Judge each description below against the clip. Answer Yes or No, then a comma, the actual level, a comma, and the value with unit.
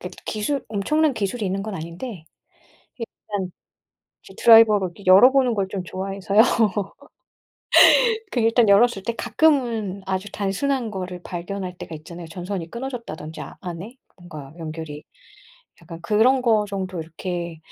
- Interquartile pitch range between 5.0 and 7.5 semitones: No, average, 4.4 semitones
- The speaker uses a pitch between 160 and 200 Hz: Yes, high, 195 Hz